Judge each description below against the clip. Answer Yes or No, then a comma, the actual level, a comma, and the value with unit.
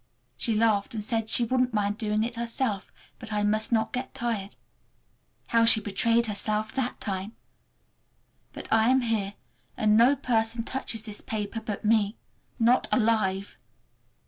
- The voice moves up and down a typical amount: No, narrow, 1.9 semitones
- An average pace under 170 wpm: Yes, average, 145 wpm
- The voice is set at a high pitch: Yes, high, 220 Hz